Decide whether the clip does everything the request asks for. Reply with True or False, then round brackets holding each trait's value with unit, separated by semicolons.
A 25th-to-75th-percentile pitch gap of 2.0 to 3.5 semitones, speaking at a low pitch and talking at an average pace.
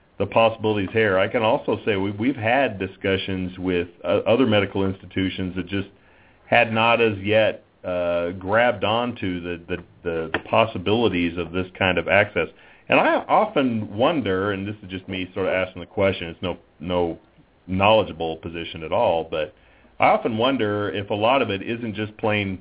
True (2.9 semitones; 95 Hz; 180 wpm)